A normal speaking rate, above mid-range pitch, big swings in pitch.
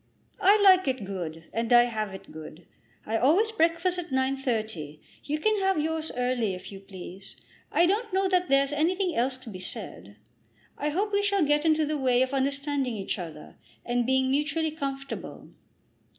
Yes: average, 180 wpm; very high, 275 Hz; wide, 6.8 semitones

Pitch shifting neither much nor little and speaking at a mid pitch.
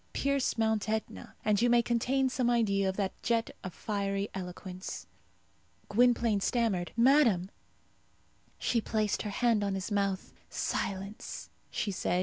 No: average, 3.3 semitones; high, 210 Hz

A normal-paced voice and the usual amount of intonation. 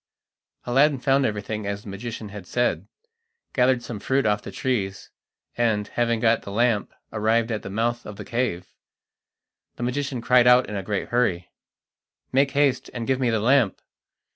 Yes: average, 170 wpm; average, 3.3 semitones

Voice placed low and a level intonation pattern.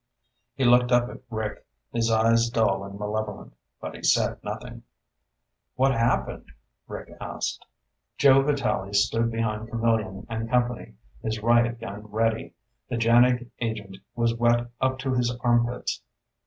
Yes: low, 115 Hz; narrow, 1.7 semitones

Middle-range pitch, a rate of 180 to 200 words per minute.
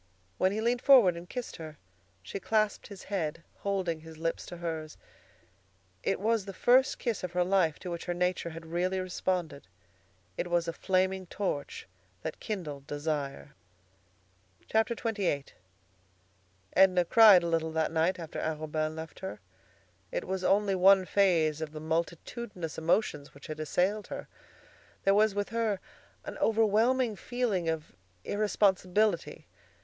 No: medium, 180 Hz; average, 145 wpm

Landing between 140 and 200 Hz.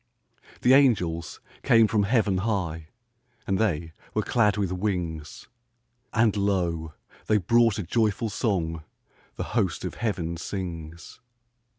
No: very low, 95 Hz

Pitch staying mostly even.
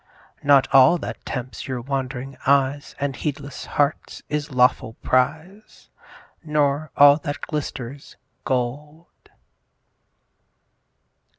Yes: narrow, 2.3 semitones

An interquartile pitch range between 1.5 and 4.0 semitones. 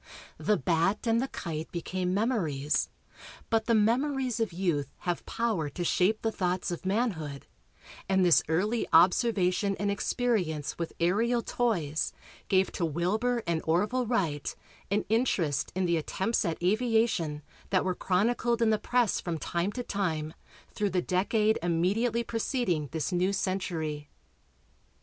No: average, 5.1 semitones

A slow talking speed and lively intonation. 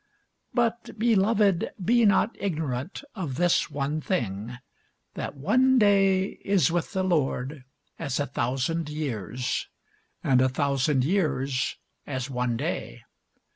Yes: slow, 120 wpm; wide, 7.0 semitones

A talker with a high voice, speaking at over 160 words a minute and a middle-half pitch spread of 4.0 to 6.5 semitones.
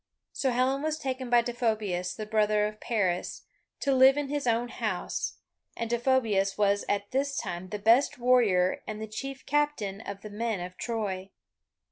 Yes: high, 225 Hz; average, 170 wpm; average, 4.3 semitones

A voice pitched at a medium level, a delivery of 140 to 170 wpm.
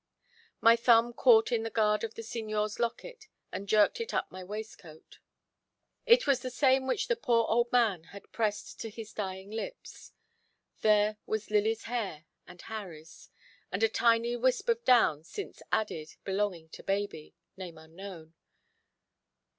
No: high, 215 Hz; average, 155 wpm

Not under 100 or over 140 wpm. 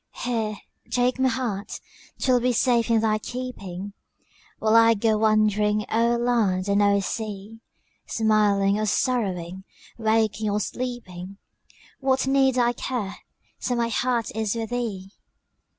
Yes: slow, 135 wpm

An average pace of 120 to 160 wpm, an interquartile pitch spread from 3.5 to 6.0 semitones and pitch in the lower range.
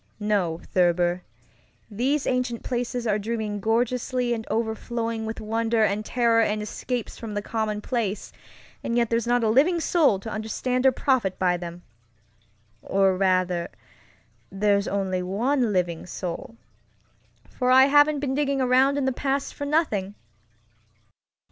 No: slow, 135 wpm; average, 4.0 semitones; high, 225 Hz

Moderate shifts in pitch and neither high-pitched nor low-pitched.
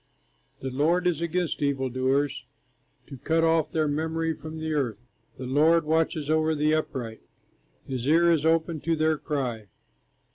Yes: average, 3.2 semitones; medium, 155 Hz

